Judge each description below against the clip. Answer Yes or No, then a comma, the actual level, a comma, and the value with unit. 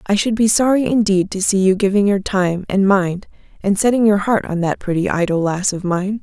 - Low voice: No, high, 200 Hz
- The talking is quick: Yes, fast, 230 wpm